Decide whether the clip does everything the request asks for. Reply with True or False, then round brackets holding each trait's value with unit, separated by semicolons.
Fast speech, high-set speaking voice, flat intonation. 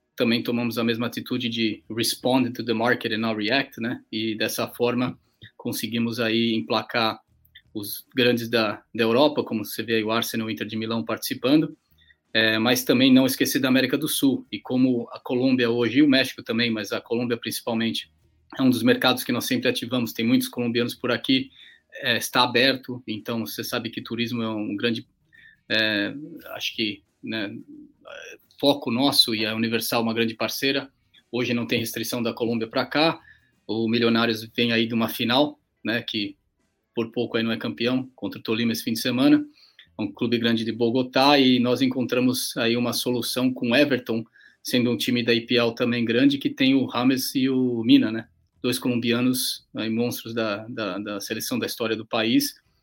False (190 wpm; 120 Hz; 2.2 semitones)